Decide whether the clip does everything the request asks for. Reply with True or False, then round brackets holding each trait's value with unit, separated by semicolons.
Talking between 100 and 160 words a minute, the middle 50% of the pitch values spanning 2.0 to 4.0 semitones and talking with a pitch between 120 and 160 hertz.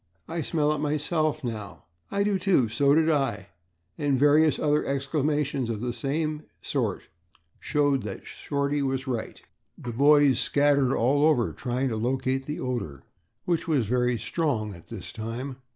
True (155 wpm; 3.4 semitones; 140 Hz)